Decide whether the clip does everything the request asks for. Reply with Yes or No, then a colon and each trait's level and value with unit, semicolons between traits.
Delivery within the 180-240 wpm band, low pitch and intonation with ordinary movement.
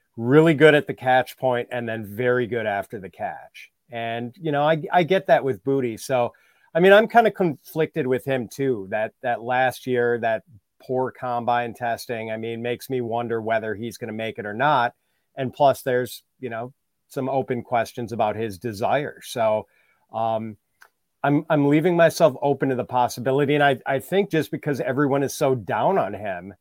Yes: average, 190 wpm; low, 125 Hz; average, 3.4 semitones